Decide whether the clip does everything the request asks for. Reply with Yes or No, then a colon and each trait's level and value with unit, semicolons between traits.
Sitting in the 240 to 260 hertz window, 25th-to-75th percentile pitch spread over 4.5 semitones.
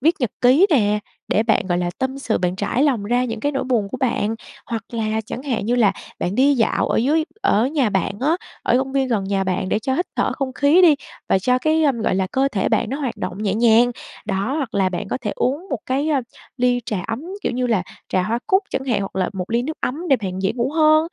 Yes: high, 245 Hz; average, 4.9 semitones